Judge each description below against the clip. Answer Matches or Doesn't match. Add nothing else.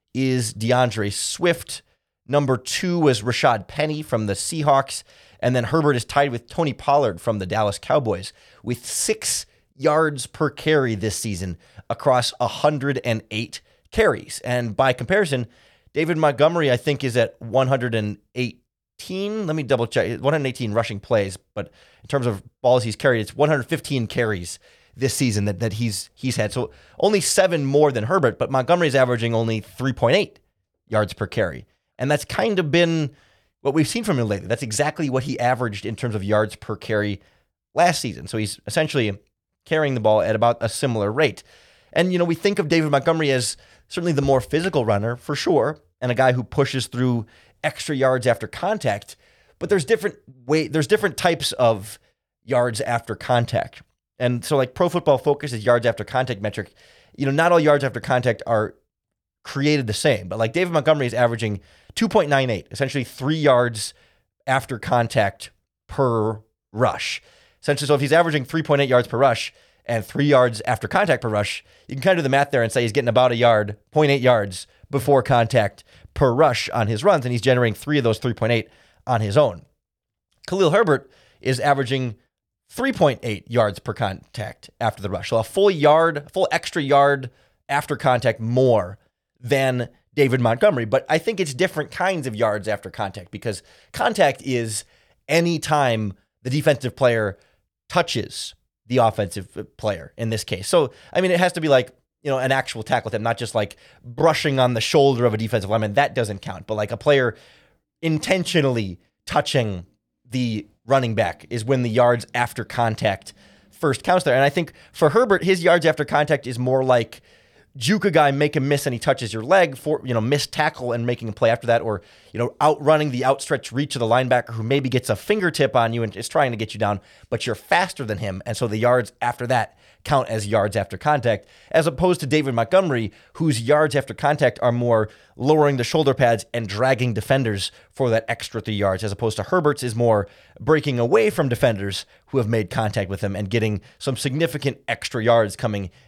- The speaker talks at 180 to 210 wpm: Matches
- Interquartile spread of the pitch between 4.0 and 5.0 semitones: Matches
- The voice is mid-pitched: Doesn't match